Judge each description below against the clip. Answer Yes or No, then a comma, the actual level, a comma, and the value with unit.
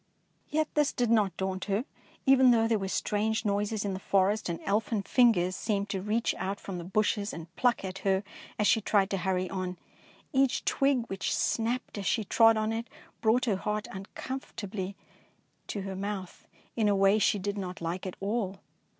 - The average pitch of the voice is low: No, high, 205 Hz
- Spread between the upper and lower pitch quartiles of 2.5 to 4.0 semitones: Yes, average, 2.9 semitones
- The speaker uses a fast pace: No, average, 190 wpm